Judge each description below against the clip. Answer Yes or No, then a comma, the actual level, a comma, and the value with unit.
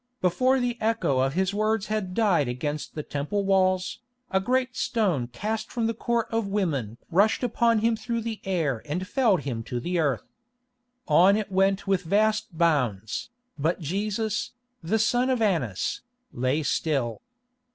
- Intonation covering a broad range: Yes, wide, 6.6 semitones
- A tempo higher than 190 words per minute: No, average, 160 wpm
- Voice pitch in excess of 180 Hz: Yes, high, 190 Hz